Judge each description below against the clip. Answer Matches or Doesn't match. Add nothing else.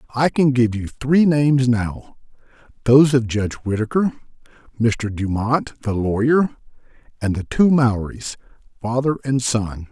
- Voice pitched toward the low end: Matches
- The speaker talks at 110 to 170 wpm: Matches